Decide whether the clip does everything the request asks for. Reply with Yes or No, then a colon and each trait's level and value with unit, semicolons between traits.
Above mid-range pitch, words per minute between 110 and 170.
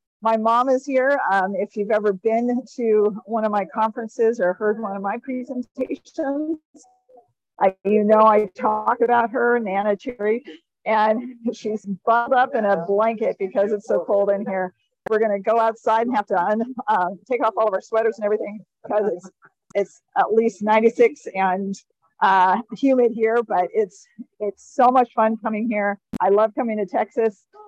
No: high, 220 Hz; average, 180 wpm